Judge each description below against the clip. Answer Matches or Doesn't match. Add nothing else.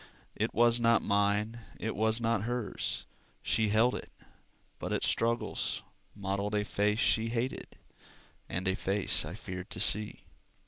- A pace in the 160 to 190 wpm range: Doesn't match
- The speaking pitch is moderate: Doesn't match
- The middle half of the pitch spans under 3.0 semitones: Matches